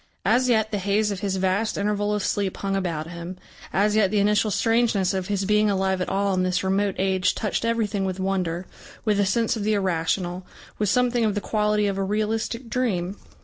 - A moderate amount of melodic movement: No, narrow, 2.1 semitones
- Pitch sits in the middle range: No, high, 200 Hz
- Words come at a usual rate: No, fast, 210 wpm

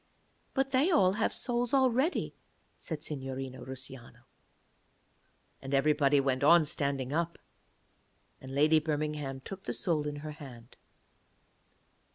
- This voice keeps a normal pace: No, slow, 120 wpm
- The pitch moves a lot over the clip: No, average, 5.0 semitones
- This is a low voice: No, medium, 150 Hz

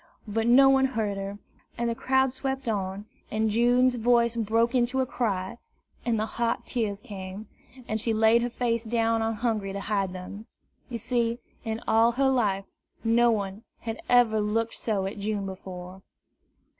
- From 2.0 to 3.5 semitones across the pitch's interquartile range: Yes, average, 2.7 semitones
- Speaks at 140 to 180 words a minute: Yes, average, 170 wpm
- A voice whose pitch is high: Yes, high, 225 Hz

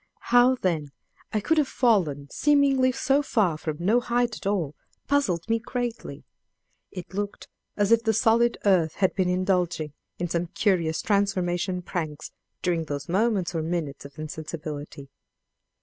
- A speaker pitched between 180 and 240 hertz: Yes, medium, 185 Hz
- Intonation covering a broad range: Yes, wide, 6.2 semitones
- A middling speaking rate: Yes, average, 150 wpm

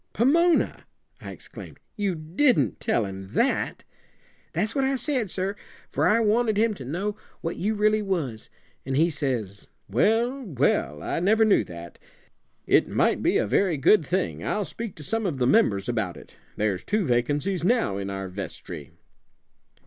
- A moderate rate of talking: Yes, average, 165 wpm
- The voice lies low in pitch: No, medium, 175 Hz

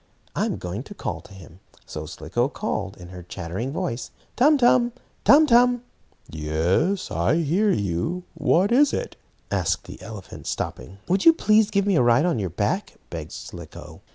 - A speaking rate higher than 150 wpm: Yes, average, 170 wpm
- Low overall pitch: Yes, low, 130 Hz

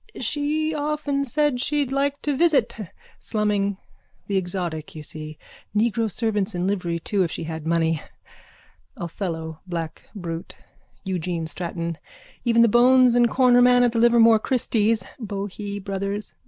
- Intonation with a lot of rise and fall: Yes, wide, 6.0 semitones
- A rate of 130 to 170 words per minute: Yes, average, 140 wpm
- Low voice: No, high, 210 Hz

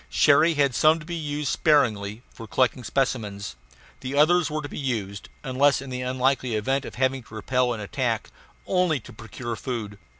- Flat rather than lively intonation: No, average, 4.5 semitones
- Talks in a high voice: No, low, 130 Hz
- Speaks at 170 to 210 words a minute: Yes, average, 180 wpm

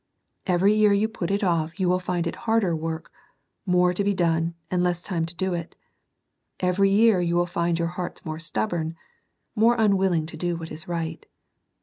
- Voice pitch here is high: No, medium, 175 Hz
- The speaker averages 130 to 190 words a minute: No, fast, 205 wpm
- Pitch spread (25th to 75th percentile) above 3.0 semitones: No, average, 2.7 semitones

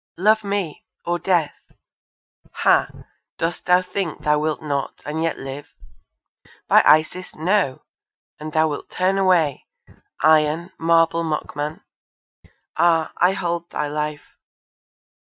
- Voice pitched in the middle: Yes, medium, 165 Hz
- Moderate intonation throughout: Yes, average, 3.0 semitones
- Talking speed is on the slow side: Yes, slow, 120 wpm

